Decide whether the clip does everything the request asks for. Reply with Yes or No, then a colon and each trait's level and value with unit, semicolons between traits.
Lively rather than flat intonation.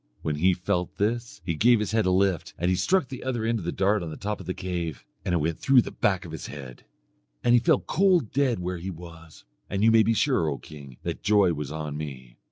Yes: wide, 5.7 semitones